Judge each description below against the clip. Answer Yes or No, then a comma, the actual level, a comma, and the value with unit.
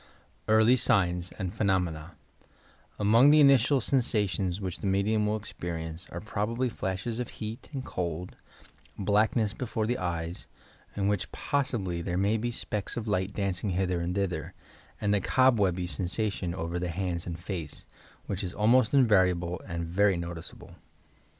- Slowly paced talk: No, average, 155 wpm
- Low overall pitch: Yes, low, 100 Hz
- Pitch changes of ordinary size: Yes, average, 3.8 semitones